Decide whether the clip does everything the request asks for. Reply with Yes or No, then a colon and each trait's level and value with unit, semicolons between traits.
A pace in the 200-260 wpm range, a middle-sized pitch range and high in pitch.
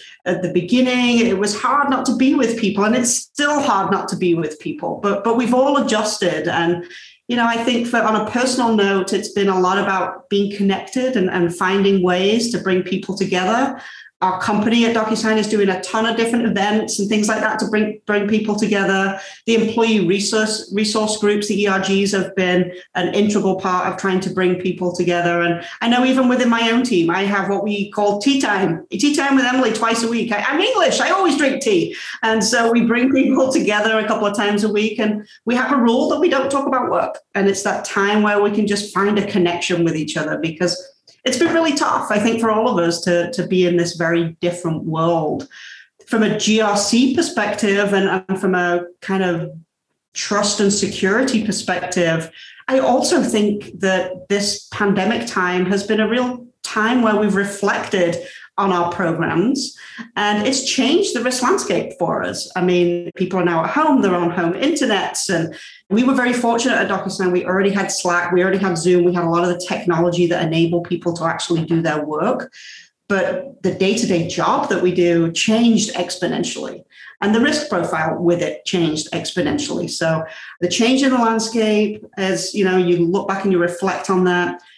Yes: fast, 205 wpm; average, 4.2 semitones; high, 200 Hz